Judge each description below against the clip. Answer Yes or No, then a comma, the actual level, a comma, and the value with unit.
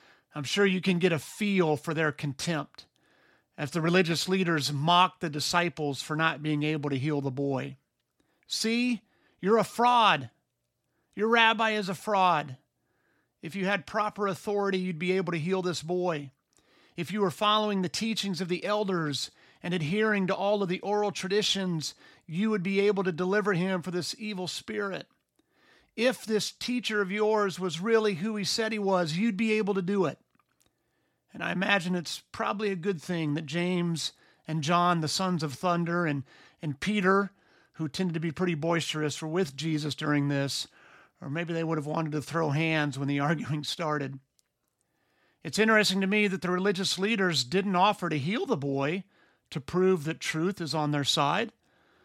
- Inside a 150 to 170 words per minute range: No, average, 180 wpm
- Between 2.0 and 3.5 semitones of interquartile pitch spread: No, average, 4.5 semitones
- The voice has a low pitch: No, medium, 180 Hz